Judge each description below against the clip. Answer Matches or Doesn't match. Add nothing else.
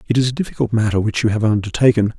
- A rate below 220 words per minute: Doesn't match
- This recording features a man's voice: Matches